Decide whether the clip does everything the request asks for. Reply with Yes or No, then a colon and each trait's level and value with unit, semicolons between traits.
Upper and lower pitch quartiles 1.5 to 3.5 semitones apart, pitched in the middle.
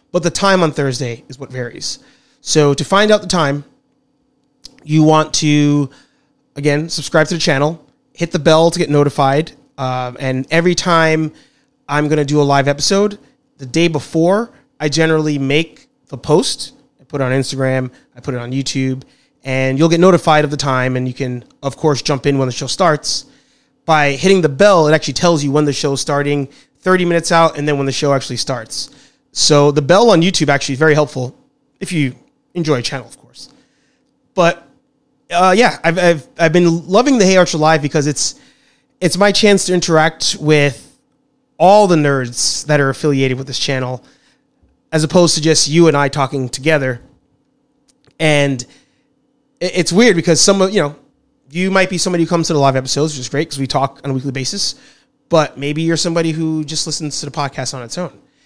No: average, 4.8 semitones; medium, 155 Hz